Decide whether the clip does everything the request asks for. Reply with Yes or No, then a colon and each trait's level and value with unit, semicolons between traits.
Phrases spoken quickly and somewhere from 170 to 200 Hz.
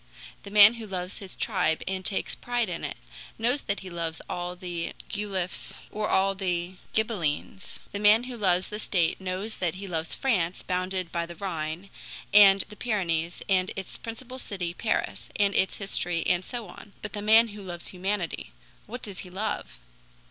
No: average, 180 wpm; high, 190 Hz